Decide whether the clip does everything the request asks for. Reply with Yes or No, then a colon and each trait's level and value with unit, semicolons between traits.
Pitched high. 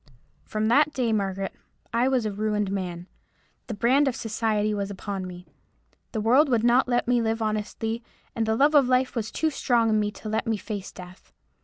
Yes: high, 220 Hz